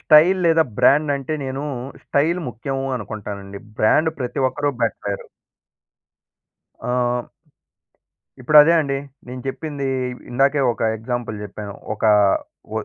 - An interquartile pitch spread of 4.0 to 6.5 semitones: Yes, average, 4.5 semitones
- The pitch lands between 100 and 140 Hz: Yes, low, 135 Hz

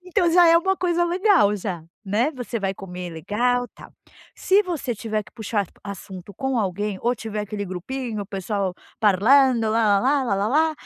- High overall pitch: Yes, high, 220 Hz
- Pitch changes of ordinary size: No, wide, 5.7 semitones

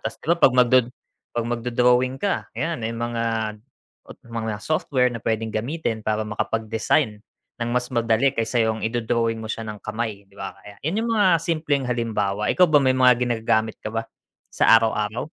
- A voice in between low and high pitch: No, low, 115 Hz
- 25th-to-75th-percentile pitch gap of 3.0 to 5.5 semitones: No, narrow, 2.4 semitones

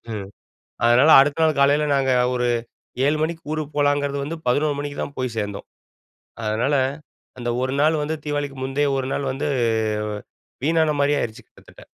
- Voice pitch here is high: No, medium, 140 Hz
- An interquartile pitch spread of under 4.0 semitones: Yes, narrow, 2.4 semitones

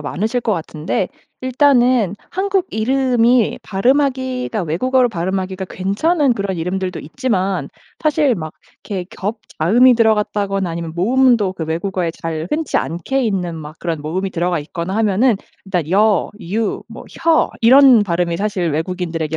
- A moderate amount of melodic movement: No, wide, 6.3 semitones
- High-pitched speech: Yes, high, 195 Hz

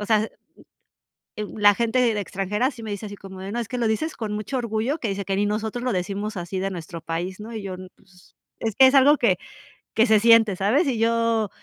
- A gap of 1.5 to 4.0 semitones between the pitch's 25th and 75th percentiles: Yes, average, 3.0 semitones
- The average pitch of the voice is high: Yes, high, 215 Hz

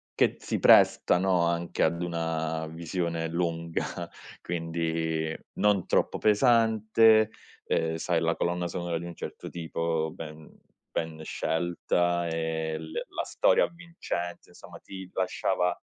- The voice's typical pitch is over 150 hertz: No, very low, 85 Hz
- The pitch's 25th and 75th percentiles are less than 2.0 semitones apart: Yes, narrow, 1.6 semitones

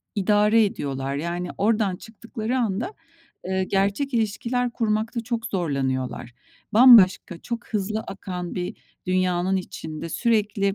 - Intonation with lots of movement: No, average, 4.1 semitones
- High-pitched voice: Yes, high, 200 Hz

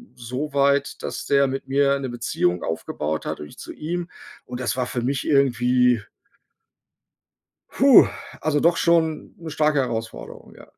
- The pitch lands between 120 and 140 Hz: Yes, low, 135 Hz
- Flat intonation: No, average, 3.4 semitones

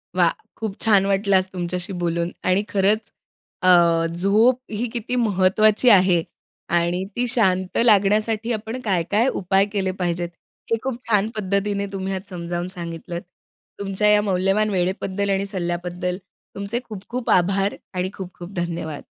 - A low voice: No, high, 195 Hz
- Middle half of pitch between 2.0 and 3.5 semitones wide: Yes, average, 2.8 semitones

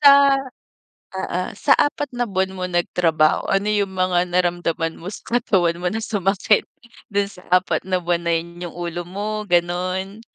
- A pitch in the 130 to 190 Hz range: Yes, medium, 185 Hz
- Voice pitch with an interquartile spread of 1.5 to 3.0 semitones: Yes, narrow, 2.6 semitones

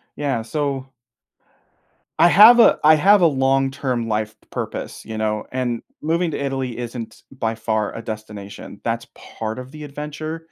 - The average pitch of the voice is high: No, low, 130 Hz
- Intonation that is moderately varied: Yes, average, 5.0 semitones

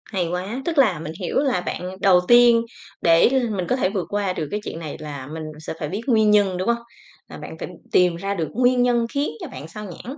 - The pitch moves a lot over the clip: Yes, wide, 5.9 semitones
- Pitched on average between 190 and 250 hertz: Yes, high, 200 Hz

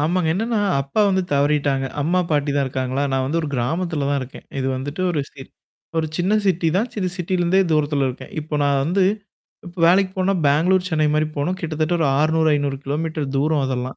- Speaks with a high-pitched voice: No, medium, 155 Hz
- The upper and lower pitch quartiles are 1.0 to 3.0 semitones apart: No, average, 3.8 semitones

